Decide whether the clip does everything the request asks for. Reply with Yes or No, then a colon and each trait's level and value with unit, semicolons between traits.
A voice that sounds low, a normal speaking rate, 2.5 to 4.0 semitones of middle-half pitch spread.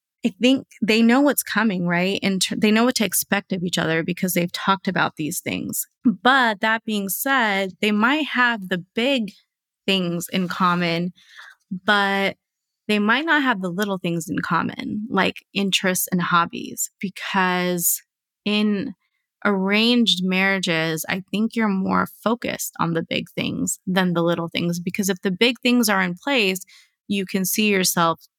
No: high, 195 Hz; average, 165 wpm; average, 3.5 semitones